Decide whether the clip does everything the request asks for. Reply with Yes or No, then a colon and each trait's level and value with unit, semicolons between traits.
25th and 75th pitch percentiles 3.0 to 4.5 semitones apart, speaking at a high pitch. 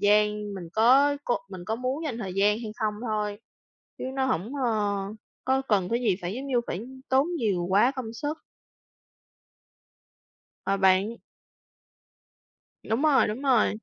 Yes: average, 4.2 semitones; high, 220 Hz